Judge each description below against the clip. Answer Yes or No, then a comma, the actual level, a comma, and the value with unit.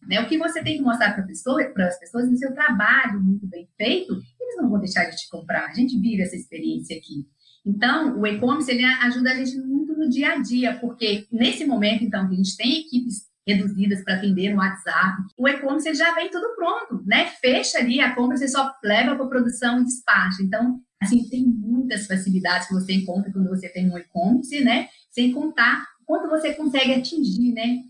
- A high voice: Yes, high, 240 Hz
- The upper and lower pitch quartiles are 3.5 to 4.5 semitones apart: No, average, 5.2 semitones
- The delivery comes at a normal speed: No, fast, 210 wpm